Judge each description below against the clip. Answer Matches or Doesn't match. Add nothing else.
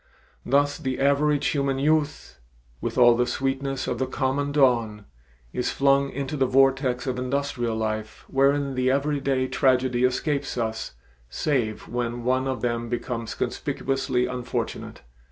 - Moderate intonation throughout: Doesn't match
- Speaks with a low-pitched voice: Matches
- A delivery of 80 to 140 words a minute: Matches